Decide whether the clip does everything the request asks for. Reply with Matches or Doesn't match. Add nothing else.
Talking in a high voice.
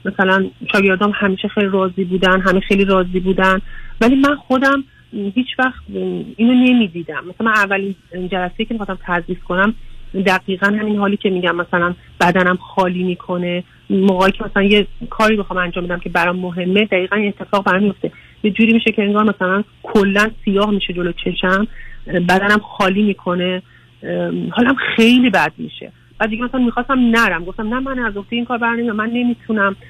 Matches